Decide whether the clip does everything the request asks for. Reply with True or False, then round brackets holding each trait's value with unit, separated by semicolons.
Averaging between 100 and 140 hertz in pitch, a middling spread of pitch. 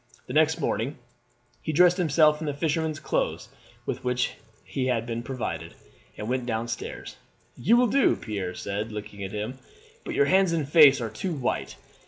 False (135 Hz; 6.0 semitones)